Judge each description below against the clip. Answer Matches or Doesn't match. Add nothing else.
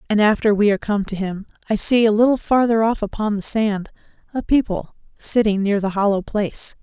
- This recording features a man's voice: Doesn't match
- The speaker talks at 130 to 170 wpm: Doesn't match